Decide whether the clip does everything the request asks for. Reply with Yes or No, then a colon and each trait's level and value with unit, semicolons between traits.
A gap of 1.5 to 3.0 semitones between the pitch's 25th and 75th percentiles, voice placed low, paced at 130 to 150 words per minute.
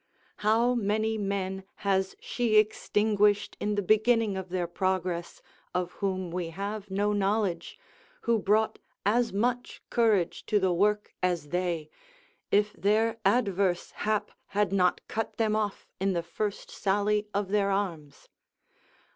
No: narrow, 2.4 semitones; high, 200 Hz; average, 140 wpm